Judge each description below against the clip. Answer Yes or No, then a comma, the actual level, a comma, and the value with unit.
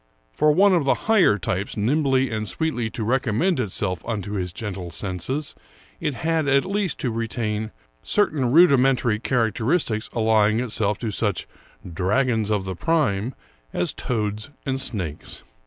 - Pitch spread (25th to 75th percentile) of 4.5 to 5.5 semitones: Yes, average, 4.8 semitones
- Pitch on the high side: No, low, 115 Hz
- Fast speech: No, average, 155 wpm